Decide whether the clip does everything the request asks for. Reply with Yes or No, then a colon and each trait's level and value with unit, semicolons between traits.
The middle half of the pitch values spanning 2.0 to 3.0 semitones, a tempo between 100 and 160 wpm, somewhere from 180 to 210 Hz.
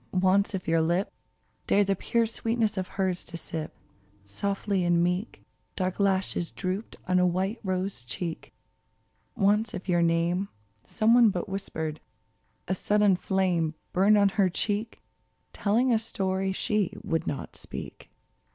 Yes: average, 2.7 semitones; average, 145 wpm; high, 190 Hz